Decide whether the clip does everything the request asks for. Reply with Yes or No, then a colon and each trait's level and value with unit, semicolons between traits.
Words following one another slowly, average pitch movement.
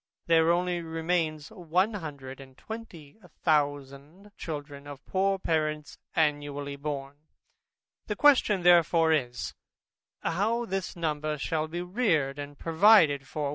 Yes: slow, 120 wpm; average, 3.7 semitones